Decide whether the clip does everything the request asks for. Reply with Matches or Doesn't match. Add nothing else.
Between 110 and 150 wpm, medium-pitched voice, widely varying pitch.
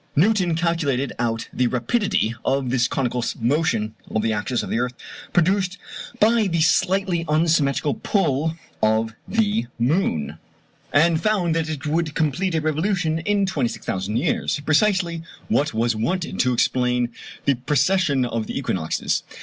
Matches